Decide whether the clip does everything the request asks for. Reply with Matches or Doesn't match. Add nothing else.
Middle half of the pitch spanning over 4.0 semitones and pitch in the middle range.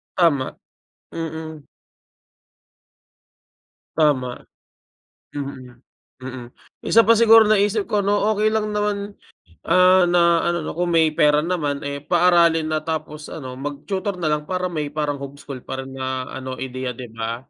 Matches